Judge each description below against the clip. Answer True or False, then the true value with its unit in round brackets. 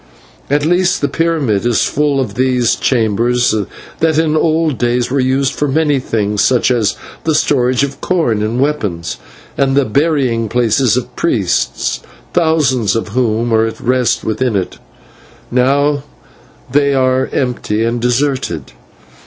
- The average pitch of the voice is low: True (130 Hz)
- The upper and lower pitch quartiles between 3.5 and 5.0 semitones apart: True (3.9 semitones)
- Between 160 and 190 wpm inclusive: False (145 wpm)